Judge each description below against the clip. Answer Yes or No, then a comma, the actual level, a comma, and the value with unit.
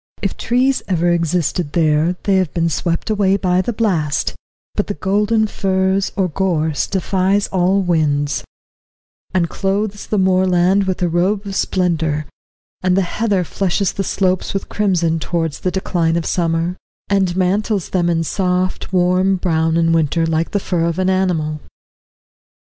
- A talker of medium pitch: Yes, medium, 180 Hz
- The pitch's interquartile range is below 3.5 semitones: Yes, narrow, 2.6 semitones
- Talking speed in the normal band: Yes, average, 155 wpm